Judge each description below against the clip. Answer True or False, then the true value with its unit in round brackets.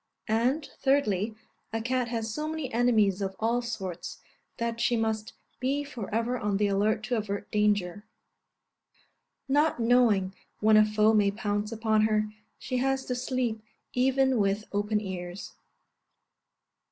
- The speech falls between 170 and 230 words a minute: False (140 wpm)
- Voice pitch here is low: False (220 Hz)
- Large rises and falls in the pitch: False (3.2 semitones)